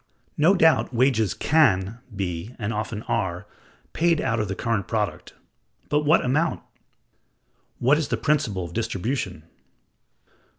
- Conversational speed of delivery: No, slow, 130 wpm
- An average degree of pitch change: No, wide, 7.3 semitones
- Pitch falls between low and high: No, low, 115 Hz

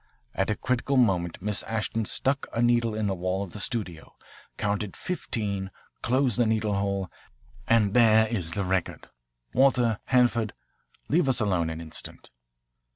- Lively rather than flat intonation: No, average, 3.7 semitones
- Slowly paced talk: No, average, 155 wpm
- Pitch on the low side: Yes, low, 110 Hz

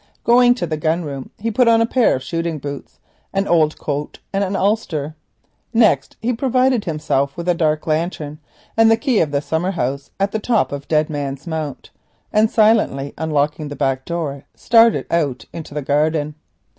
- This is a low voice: No, medium, 160 Hz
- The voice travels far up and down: Yes, wide, 6.7 semitones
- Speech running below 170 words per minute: No, average, 185 wpm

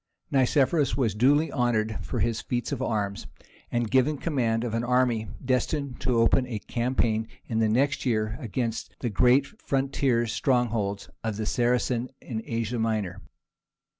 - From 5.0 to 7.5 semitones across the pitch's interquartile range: No, average, 2.7 semitones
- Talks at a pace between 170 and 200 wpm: No, average, 150 wpm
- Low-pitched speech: Yes, low, 120 Hz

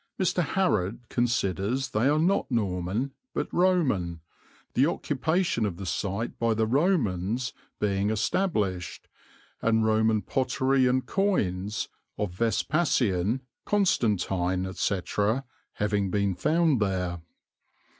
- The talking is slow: Yes, slow, 105 wpm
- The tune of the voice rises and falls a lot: Yes, wide, 5.9 semitones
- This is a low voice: Yes, low, 110 Hz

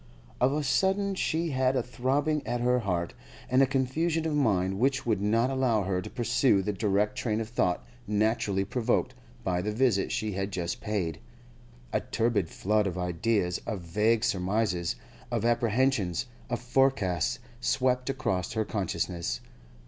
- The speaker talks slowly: No, average, 155 wpm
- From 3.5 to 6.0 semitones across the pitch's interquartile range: Yes, average, 5.1 semitones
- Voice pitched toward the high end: No, low, 110 Hz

